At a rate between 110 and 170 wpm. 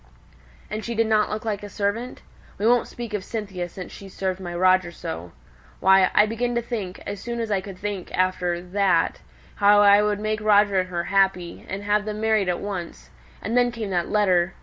No: fast, 205 wpm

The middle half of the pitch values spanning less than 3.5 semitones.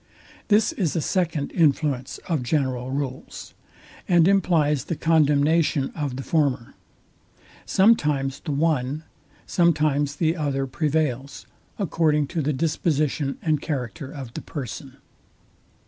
Yes: average, 3.0 semitones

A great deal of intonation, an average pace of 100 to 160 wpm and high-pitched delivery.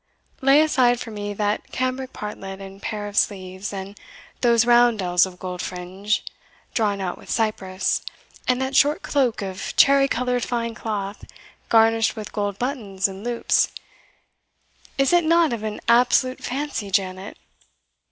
No: average, 4.3 semitones; average, 145 wpm; high, 220 Hz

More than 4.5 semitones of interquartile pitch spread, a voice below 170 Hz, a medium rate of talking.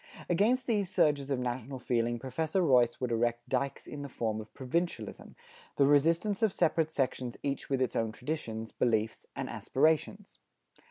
Yes: average, 5.1 semitones; low, 135 Hz; average, 160 wpm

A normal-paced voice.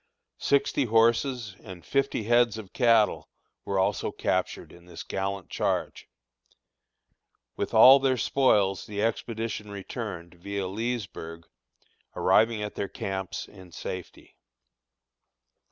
No: slow, 110 wpm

